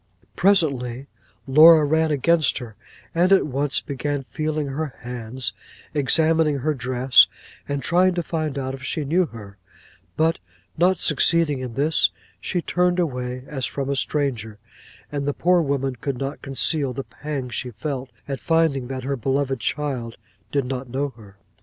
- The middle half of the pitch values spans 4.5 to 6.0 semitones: No, average, 3.5 semitones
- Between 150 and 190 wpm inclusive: Yes, average, 160 wpm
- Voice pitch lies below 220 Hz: Yes, medium, 140 Hz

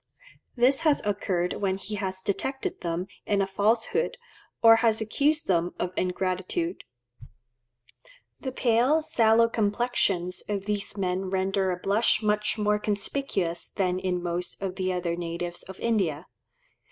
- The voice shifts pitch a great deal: No, average, 3.8 semitones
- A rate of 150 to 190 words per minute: No, average, 140 wpm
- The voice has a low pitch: No, high, 200 Hz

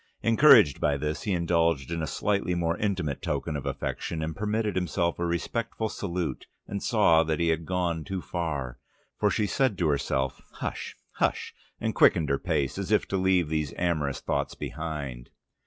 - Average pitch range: Yes, average, 4.1 semitones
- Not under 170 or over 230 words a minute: Yes, average, 175 wpm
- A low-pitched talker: Yes, very low, 85 Hz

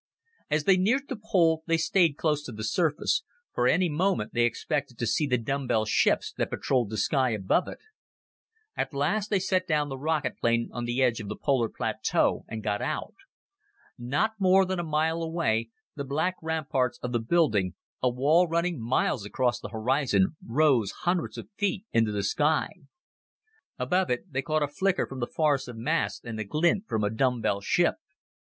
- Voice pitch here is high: No, medium, 140 Hz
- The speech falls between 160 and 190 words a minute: Yes, average, 185 wpm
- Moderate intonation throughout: No, wide, 6.0 semitones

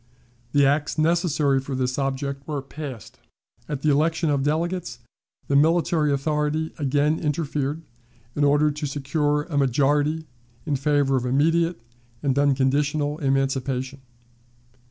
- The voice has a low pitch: No, medium, 145 Hz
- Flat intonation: Yes, narrow, 2.0 semitones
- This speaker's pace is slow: Yes, slow, 125 wpm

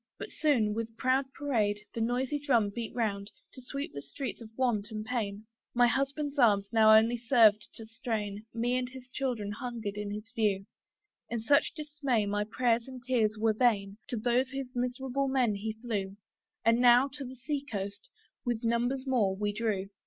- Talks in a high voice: Yes, high, 235 Hz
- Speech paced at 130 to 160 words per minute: No, average, 180 wpm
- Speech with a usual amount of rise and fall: Yes, average, 3.4 semitones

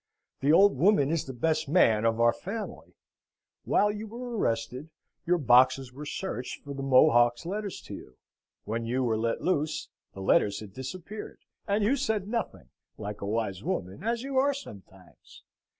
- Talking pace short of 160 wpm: No, average, 170 wpm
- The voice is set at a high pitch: No, medium, 140 Hz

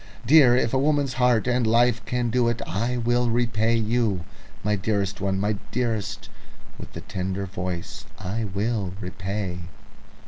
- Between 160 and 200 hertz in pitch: No, low, 110 Hz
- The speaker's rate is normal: Yes, average, 150 wpm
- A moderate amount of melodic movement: Yes, average, 3.6 semitones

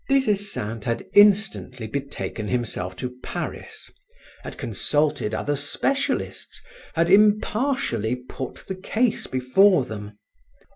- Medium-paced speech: No, slow, 105 wpm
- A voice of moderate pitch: Yes, medium, 145 Hz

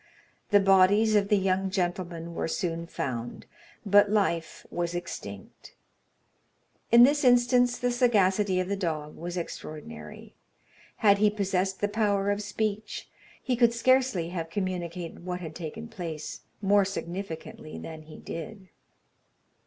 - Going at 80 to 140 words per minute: Yes, slow, 135 wpm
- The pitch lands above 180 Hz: Yes, high, 190 Hz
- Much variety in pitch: No, average, 3.7 semitones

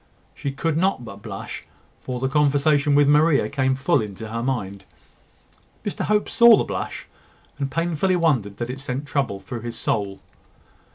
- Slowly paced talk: No, average, 165 wpm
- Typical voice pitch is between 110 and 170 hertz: Yes, low, 135 Hz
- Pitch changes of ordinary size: Yes, average, 4.4 semitones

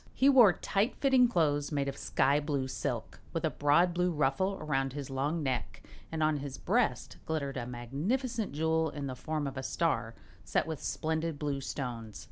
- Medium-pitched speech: Yes, medium, 150 Hz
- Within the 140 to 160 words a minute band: No, average, 185 wpm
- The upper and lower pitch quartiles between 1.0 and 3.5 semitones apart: No, average, 3.9 semitones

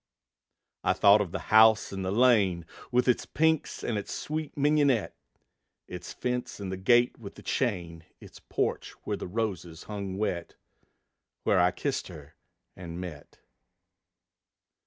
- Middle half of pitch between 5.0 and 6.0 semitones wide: Yes, wide, 5.4 semitones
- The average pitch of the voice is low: Yes, low, 100 Hz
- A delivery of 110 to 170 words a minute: Yes, average, 145 wpm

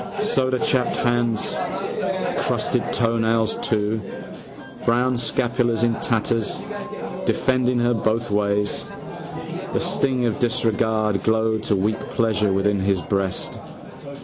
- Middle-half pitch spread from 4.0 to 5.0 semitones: No, narrow, 2.5 semitones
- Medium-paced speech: No, slow, 100 wpm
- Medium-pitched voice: No, low, 115 Hz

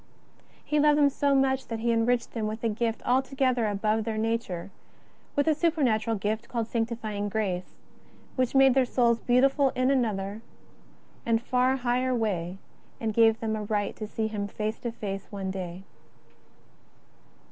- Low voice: No, high, 230 Hz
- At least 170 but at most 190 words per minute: No, average, 160 wpm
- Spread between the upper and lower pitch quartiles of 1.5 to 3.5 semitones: Yes, average, 3.1 semitones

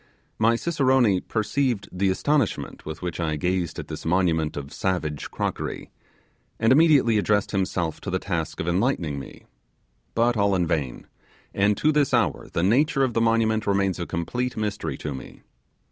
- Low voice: Yes, low, 100 Hz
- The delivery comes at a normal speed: Yes, average, 165 wpm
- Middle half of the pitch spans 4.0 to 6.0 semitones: Yes, wide, 5.6 semitones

